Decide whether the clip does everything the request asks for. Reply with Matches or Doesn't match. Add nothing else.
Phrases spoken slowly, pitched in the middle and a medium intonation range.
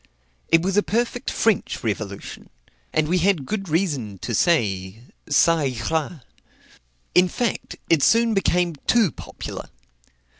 Doesn't match